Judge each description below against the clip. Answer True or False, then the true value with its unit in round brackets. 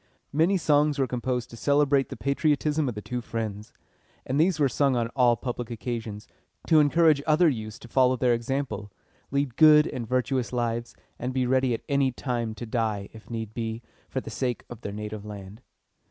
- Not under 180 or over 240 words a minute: True (190 wpm)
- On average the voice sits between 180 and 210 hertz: False (125 Hz)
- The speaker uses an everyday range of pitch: True (3.6 semitones)